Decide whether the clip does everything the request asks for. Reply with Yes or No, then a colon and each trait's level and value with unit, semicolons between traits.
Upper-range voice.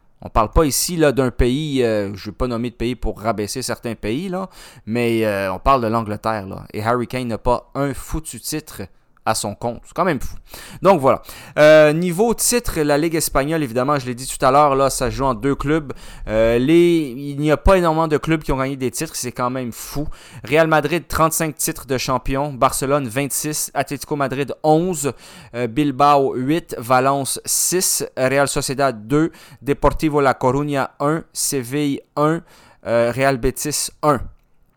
No: medium, 140 Hz